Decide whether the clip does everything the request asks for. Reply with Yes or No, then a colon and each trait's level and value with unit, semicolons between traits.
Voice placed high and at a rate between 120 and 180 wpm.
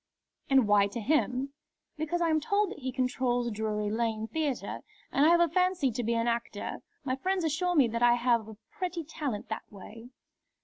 No: very high, 255 Hz; average, 195 wpm